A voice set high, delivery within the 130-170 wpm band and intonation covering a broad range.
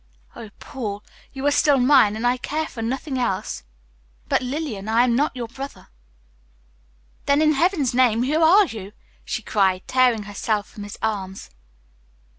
No: high, 245 Hz; average, 160 wpm; average, 4.8 semitones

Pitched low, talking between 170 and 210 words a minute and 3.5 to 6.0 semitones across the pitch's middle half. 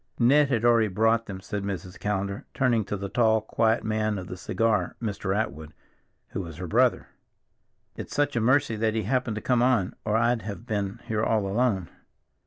No: low, 110 Hz; average, 195 wpm; average, 2.9 semitones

